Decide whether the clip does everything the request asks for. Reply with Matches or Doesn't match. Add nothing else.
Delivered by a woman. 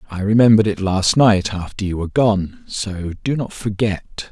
Doesn't match